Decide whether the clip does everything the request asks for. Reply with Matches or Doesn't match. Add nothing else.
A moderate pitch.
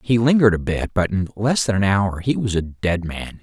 Doesn't match